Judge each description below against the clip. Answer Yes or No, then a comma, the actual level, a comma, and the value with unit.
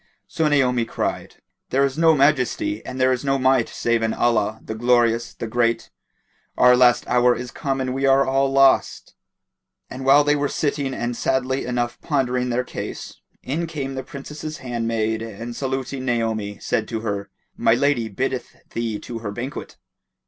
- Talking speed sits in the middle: Yes, average, 170 wpm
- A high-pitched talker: No, low, 125 Hz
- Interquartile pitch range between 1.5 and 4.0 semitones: Yes, narrow, 2.6 semitones